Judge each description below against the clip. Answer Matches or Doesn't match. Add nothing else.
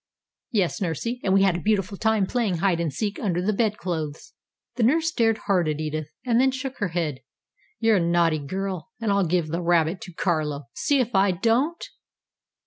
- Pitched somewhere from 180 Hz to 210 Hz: Matches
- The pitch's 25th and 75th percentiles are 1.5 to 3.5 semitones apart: Doesn't match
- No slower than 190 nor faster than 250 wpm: Matches